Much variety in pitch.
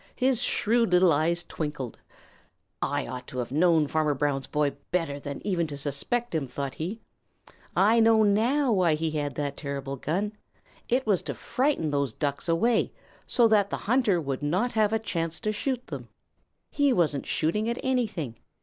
Yes: wide, 7.3 semitones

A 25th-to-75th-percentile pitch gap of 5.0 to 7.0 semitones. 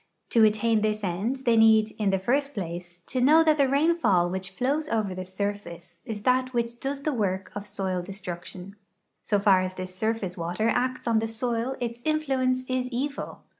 Yes: average, 5.3 semitones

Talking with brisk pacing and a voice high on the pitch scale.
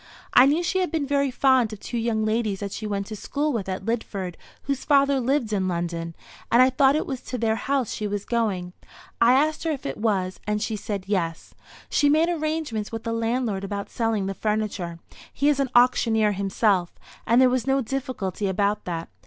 Yes: fast, 210 wpm; high, 225 Hz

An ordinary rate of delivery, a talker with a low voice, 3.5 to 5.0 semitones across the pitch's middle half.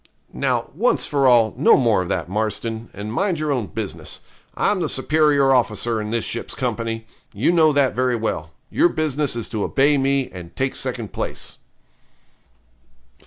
Yes: average, 165 wpm; low, 125 Hz; average, 4.4 semitones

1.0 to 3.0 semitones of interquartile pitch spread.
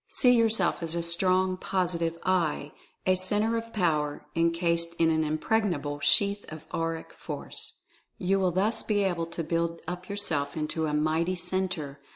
Yes: average, 2.7 semitones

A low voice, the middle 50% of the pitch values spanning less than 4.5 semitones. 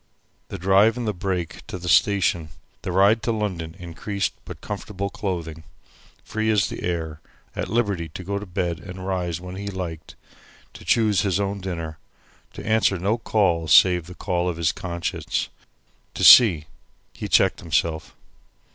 Yes: very low, 95 Hz; average, 3.0 semitones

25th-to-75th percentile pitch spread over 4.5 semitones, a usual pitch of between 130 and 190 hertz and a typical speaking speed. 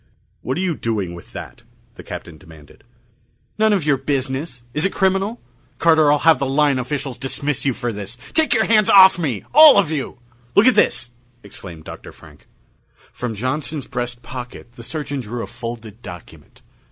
Yes: average, 5.3 semitones; low, 135 Hz; average, 175 wpm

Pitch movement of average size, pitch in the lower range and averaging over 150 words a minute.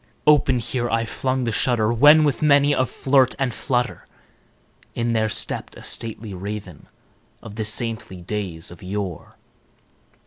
No: average, 3.9 semitones; low, 115 Hz; average, 145 wpm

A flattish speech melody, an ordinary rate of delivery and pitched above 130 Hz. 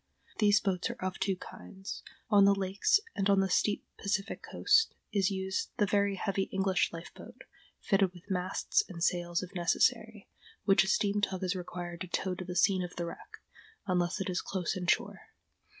Yes: narrow, 1.8 semitones; average, 190 wpm; high, 190 Hz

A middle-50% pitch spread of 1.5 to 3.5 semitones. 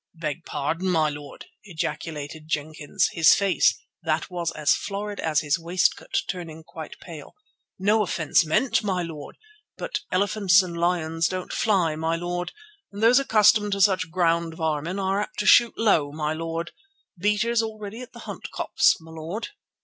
No: average, 3.9 semitones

